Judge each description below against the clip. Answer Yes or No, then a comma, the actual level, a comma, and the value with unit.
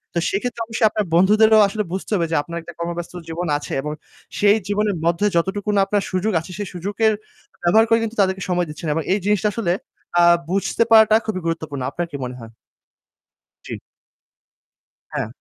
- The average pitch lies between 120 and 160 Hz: No, high, 190 Hz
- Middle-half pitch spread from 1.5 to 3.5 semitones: No, average, 4.0 semitones